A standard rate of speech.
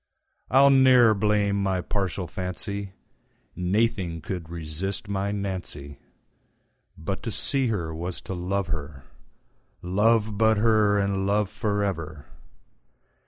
No: slow, 105 wpm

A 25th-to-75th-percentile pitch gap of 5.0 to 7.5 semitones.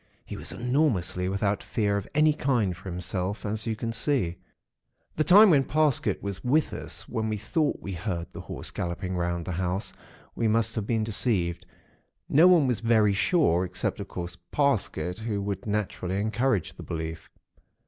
Yes: average, 5.3 semitones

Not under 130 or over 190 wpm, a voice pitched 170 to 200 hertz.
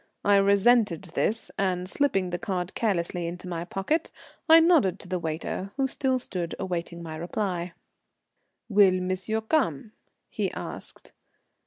Yes: average, 140 wpm; high, 190 Hz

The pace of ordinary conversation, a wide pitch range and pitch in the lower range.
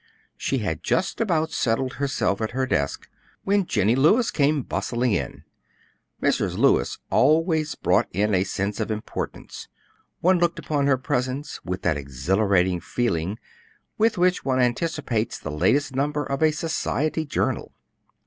Yes: average, 145 wpm; wide, 7.1 semitones; low, 130 Hz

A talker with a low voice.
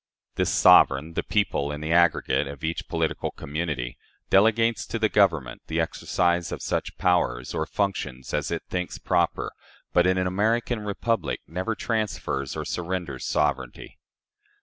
Yes: very low, 85 Hz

